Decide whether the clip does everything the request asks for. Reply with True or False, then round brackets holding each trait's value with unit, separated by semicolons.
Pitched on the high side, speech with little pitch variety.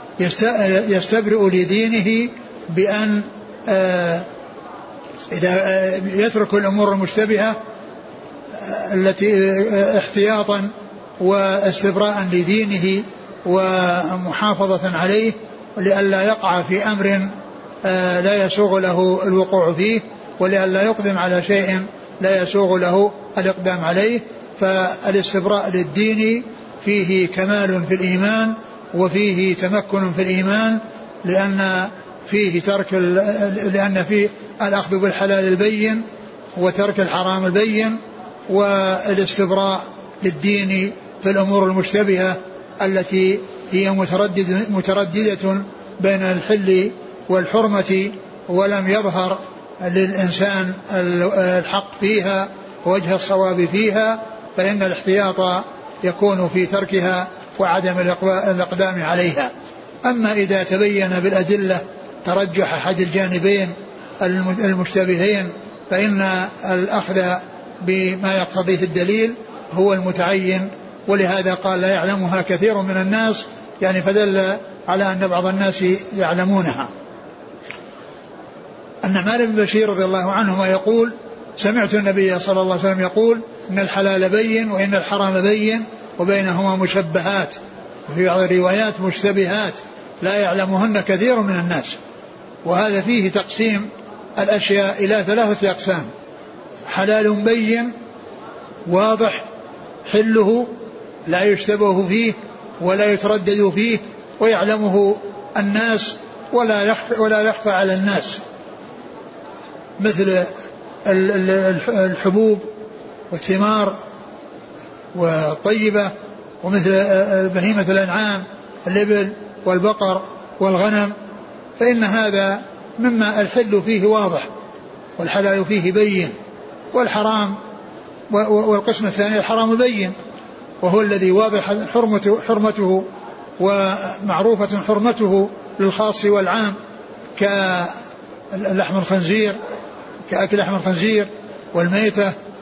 True (195 Hz; 1.9 semitones)